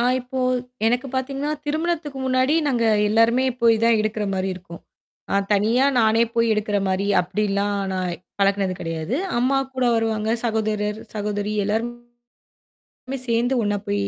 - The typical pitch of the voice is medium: No, high, 225 Hz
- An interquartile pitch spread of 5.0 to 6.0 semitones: No, average, 3.4 semitones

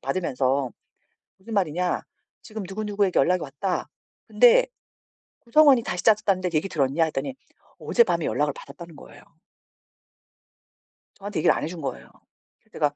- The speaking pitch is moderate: Yes, medium, 180 Hz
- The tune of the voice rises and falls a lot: Yes, wide, 5.9 semitones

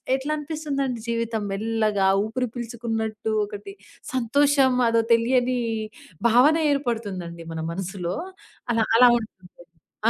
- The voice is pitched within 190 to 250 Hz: Yes, high, 230 Hz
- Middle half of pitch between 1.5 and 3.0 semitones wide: No, average, 3.4 semitones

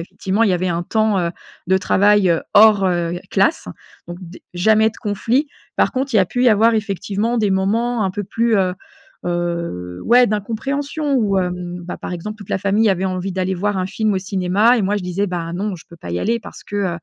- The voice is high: Yes, high, 195 Hz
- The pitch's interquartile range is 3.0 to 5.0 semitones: Yes, average, 3.4 semitones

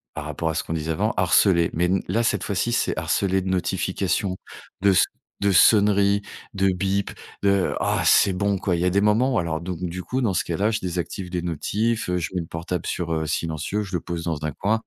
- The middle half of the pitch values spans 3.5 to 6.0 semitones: No, average, 3.0 semitones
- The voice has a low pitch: Yes, very low, 90 Hz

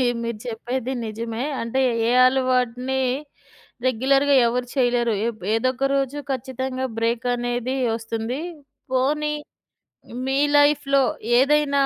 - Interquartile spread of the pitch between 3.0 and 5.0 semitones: No, narrow, 2.4 semitones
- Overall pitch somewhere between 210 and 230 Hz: No, very high, 255 Hz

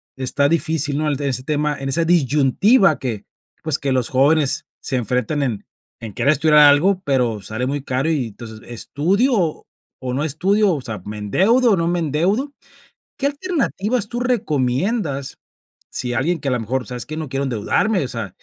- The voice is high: No, medium, 145 Hz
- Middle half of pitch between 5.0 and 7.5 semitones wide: Yes, wide, 5.5 semitones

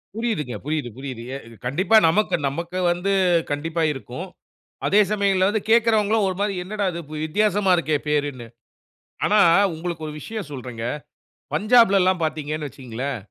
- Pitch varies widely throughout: Yes, wide, 6.1 semitones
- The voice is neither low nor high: Yes, medium, 170 Hz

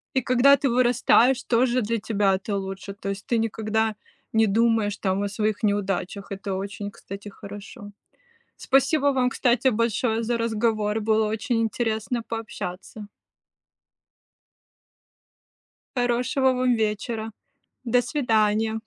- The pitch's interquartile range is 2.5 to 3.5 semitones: Yes, average, 2.8 semitones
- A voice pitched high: Yes, high, 220 Hz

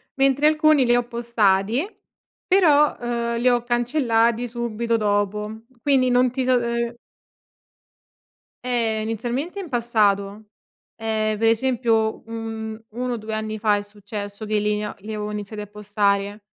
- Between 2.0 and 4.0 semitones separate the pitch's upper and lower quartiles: Yes, narrow, 2.5 semitones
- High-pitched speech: Yes, high, 225 Hz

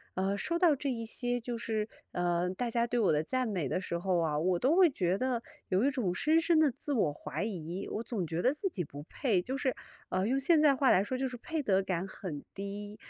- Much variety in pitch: Yes, wide, 6.2 semitones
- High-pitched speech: Yes, high, 220 Hz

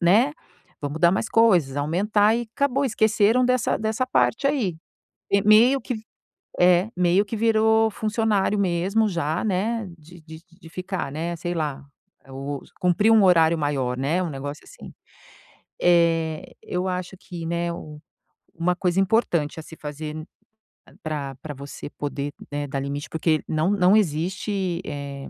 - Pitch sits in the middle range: Yes, medium, 175 Hz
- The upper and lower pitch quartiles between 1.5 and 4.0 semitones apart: No, wide, 5.4 semitones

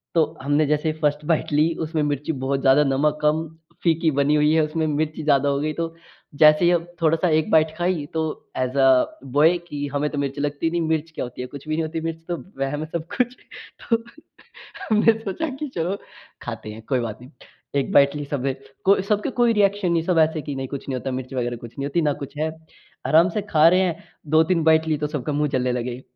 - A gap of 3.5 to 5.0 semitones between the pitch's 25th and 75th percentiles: No, average, 2.8 semitones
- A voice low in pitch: No, medium, 155 Hz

